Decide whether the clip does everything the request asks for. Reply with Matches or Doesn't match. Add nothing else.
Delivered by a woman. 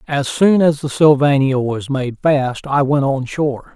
Doesn't match